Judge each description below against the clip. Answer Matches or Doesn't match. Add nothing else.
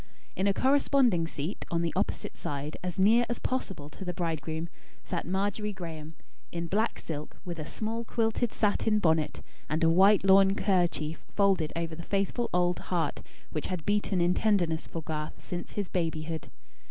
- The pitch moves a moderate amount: Matches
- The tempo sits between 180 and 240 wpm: Doesn't match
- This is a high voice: Doesn't match